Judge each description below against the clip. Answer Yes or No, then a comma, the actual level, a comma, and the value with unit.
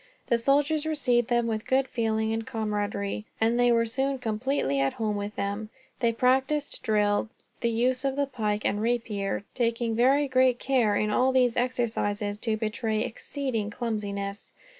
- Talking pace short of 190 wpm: Yes, average, 160 wpm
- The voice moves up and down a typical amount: Yes, average, 3.3 semitones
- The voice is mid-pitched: No, high, 230 Hz